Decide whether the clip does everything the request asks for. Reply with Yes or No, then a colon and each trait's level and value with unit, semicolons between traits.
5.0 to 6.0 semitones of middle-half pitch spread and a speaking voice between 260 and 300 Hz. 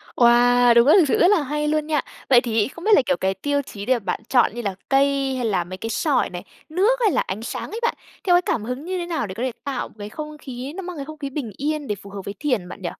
Yes: average, 5.3 semitones; very high, 265 Hz